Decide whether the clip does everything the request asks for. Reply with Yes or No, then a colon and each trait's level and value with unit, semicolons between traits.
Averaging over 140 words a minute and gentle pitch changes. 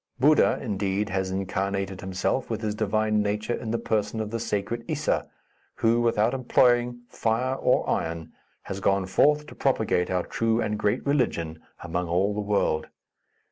No: average, 160 wpm; average, 3.5 semitones